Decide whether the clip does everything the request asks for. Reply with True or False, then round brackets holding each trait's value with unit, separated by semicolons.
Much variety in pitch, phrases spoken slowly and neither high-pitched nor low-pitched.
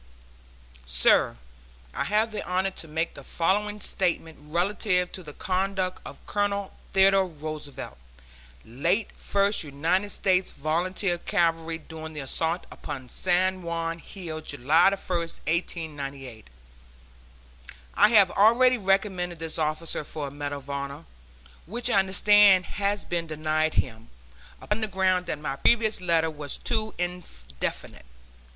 False (3.9 semitones; 130 wpm; 175 Hz)